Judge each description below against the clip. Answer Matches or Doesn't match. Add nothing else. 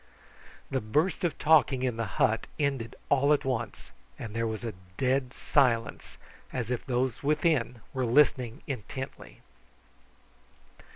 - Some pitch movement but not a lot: Matches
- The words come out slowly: Matches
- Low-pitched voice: Matches